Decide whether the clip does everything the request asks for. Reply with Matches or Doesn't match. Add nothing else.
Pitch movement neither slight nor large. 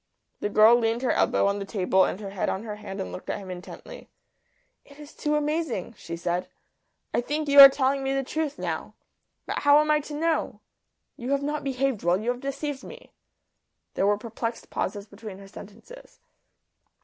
Doesn't match